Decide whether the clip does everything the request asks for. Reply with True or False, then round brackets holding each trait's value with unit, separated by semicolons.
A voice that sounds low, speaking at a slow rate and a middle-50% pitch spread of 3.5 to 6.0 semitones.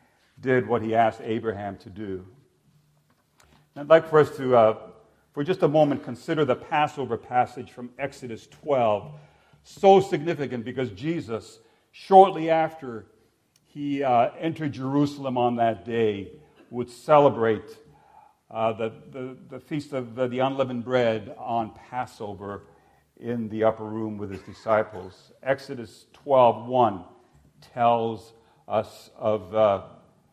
True (120 Hz; 130 wpm; 4.5 semitones)